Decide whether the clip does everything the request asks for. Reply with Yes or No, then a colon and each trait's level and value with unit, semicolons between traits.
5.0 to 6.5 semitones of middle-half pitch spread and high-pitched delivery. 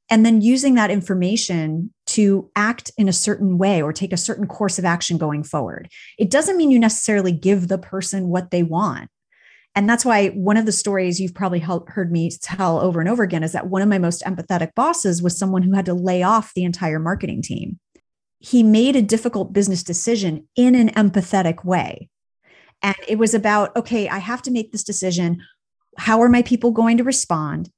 No: average, 3.8 semitones; high, 195 Hz